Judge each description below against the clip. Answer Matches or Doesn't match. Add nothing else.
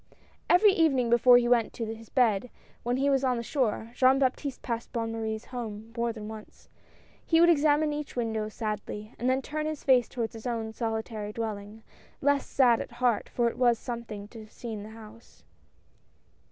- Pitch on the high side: Matches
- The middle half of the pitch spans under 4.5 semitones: Matches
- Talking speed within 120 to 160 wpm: Doesn't match